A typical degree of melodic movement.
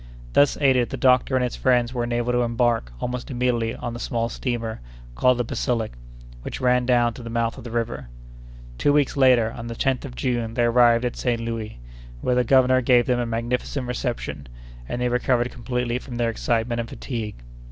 No: narrow, 1.3 semitones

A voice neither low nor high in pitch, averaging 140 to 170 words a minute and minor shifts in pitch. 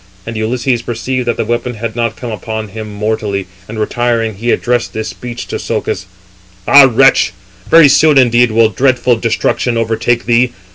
No: low, 115 Hz; average, 165 wpm; narrow, 1.9 semitones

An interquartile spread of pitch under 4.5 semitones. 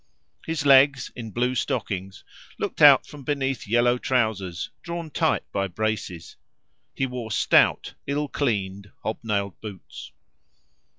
No: average, 5.2 semitones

